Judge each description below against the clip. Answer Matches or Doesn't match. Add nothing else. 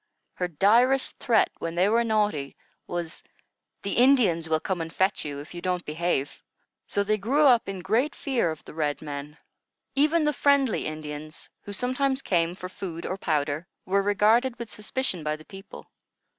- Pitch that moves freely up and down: Matches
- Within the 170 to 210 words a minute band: Matches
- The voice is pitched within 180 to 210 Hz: Matches